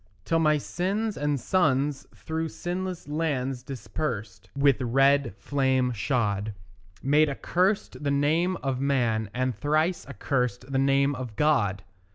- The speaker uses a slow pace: Yes, slow, 130 wpm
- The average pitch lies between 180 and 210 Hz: No, medium, 140 Hz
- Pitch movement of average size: Yes, average, 3.7 semitones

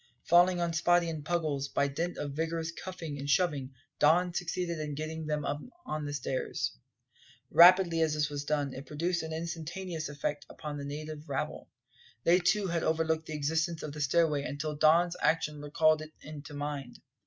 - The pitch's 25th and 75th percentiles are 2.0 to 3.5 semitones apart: Yes, narrow, 2.5 semitones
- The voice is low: No, medium, 155 Hz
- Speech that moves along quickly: No, average, 175 wpm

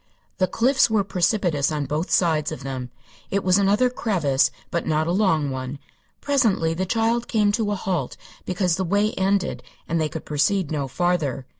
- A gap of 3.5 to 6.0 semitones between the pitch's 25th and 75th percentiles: Yes, average, 5.1 semitones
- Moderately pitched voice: Yes, medium, 180 Hz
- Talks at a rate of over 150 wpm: Yes, average, 180 wpm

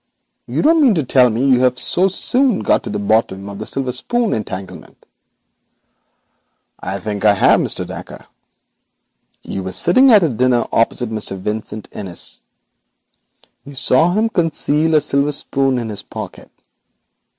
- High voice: No, low, 125 Hz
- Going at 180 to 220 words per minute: No, average, 150 wpm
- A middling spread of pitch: No, wide, 7.5 semitones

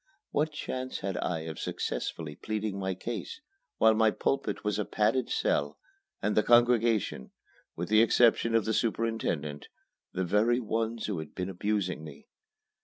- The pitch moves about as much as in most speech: Yes, average, 4.0 semitones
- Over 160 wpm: No, average, 155 wpm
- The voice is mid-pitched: No, low, 105 Hz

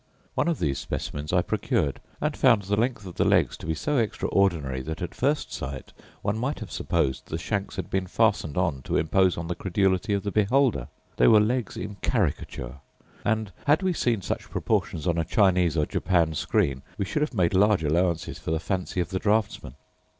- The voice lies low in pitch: Yes, very low, 95 Hz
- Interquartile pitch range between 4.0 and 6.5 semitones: Yes, average, 4.9 semitones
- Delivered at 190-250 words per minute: Yes, average, 200 wpm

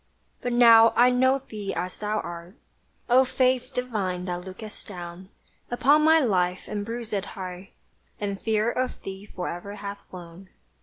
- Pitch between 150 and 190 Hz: No, high, 210 Hz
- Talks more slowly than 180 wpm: Yes, average, 150 wpm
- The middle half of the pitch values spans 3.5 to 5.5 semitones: Yes, average, 4.8 semitones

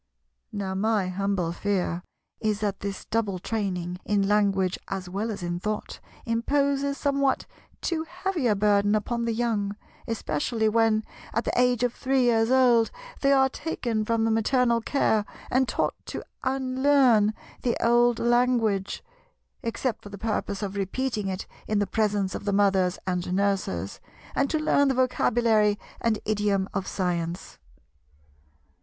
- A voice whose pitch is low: No, high, 215 Hz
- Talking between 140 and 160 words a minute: Yes, average, 145 wpm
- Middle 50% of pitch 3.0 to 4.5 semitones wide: Yes, average, 3.7 semitones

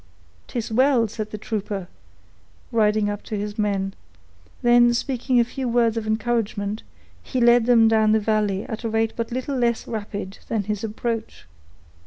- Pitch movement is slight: Yes, narrow, 2.3 semitones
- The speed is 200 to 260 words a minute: No, average, 165 wpm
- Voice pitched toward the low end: No, high, 225 Hz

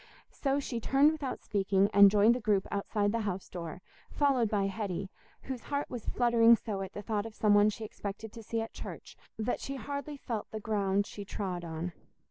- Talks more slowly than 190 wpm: No, fast, 205 wpm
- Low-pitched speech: No, high, 215 Hz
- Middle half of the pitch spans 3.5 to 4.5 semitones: No, average, 3.1 semitones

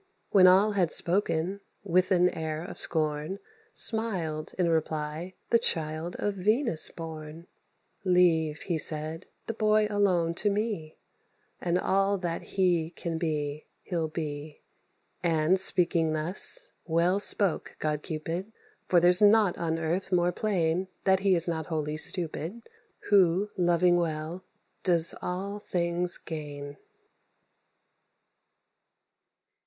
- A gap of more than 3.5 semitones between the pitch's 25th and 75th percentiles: No, average, 3.1 semitones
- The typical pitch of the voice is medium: Yes, medium, 175 Hz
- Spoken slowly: Yes, slow, 120 wpm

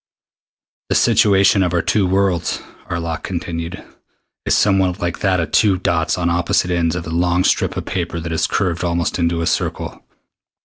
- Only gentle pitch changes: Yes, narrow, 2.0 semitones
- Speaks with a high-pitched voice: No, very low, 85 Hz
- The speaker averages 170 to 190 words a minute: Yes, average, 175 wpm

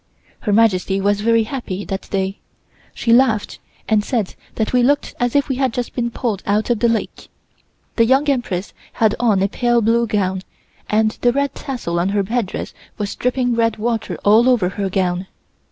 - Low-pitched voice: No, high, 225 Hz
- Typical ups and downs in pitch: Yes, average, 3.4 semitones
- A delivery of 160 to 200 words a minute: Yes, average, 185 wpm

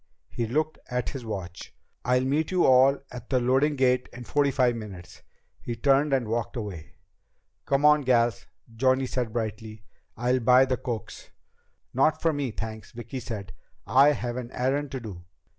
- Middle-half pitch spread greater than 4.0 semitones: No, average, 2.9 semitones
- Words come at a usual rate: Yes, average, 170 wpm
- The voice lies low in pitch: Yes, low, 125 Hz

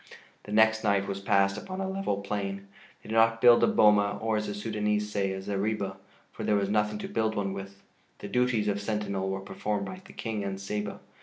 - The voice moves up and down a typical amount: No, narrow, 1.9 semitones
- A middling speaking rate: No, fast, 220 wpm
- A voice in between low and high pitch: No, low, 105 Hz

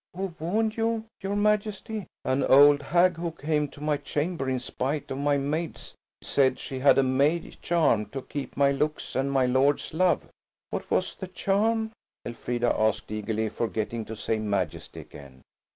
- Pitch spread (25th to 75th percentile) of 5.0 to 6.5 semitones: Yes, wide, 5.5 semitones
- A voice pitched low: No, medium, 145 Hz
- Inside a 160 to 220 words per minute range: Yes, average, 170 wpm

